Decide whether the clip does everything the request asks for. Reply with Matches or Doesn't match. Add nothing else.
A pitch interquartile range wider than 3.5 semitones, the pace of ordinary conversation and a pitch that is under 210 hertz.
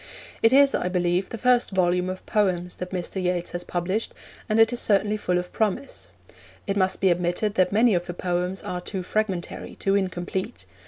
Doesn't match